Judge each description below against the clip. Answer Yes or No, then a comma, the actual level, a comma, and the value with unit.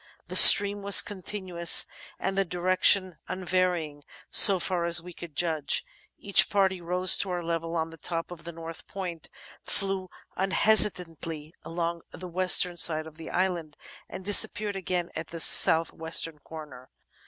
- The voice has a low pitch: No, medium, 175 Hz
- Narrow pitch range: Yes, narrow, 2.3 semitones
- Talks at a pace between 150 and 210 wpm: Yes, average, 155 wpm